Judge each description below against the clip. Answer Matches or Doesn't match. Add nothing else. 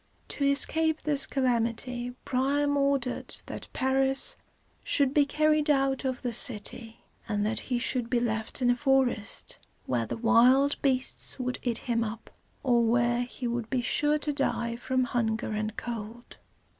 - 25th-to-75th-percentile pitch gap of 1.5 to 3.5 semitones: Matches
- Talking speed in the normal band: Matches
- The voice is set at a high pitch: Matches